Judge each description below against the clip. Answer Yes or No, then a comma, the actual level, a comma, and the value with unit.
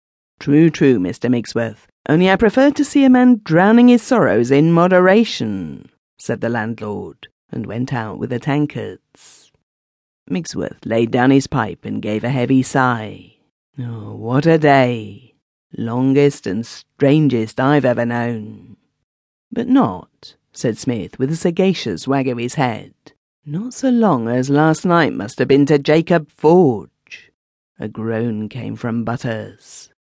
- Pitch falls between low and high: No, low, 130 Hz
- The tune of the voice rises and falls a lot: Yes, wide, 5.9 semitones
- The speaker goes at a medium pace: Yes, average, 145 wpm